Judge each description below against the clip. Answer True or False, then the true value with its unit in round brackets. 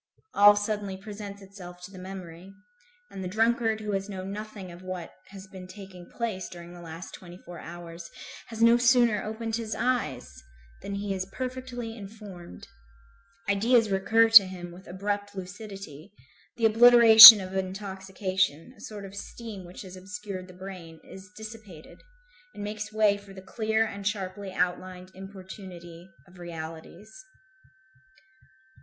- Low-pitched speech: False (195 Hz)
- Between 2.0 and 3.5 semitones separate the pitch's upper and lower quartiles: True (2.8 semitones)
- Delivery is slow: False (150 wpm)